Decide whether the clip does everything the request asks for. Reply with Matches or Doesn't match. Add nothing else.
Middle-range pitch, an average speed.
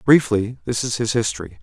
Doesn't match